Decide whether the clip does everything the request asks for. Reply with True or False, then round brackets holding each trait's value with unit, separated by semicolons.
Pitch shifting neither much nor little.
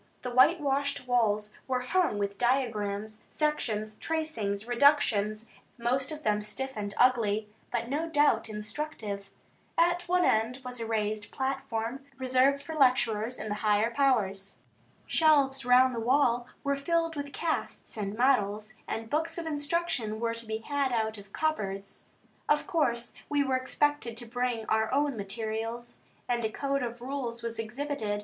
True (4.4 semitones)